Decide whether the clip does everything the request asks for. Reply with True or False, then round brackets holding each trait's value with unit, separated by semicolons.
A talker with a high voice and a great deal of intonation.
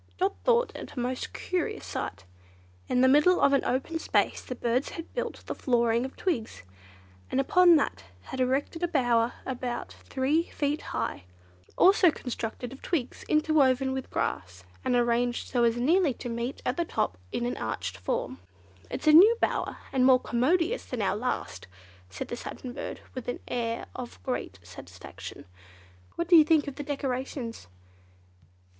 False (255 Hz; 4.5 semitones)